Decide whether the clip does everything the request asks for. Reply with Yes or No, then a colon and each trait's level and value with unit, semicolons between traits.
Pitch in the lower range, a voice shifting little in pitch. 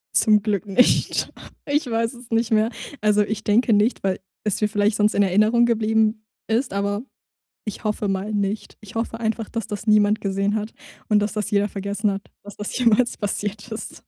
No: high, 210 Hz; narrow, 1.7 semitones